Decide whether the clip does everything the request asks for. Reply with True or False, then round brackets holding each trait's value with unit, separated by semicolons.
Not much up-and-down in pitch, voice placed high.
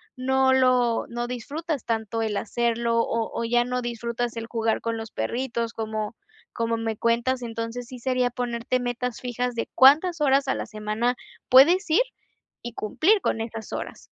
True (1.9 semitones; 240 Hz)